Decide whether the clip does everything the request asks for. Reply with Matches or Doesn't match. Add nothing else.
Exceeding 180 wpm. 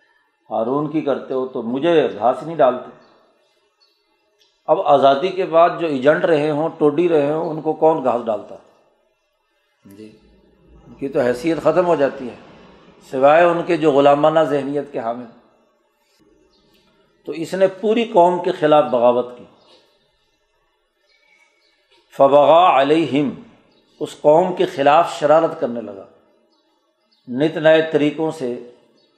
Doesn't match